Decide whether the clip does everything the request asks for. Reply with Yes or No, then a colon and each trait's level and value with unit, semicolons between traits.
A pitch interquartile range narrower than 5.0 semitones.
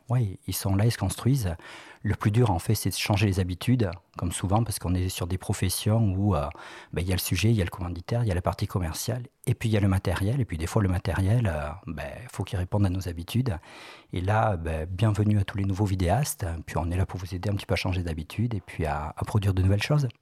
Yes: average, 3.2 semitones